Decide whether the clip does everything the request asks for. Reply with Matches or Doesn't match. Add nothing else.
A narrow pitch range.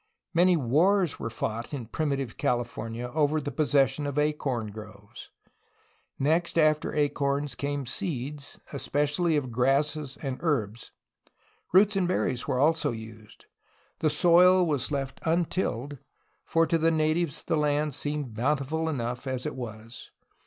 Doesn't match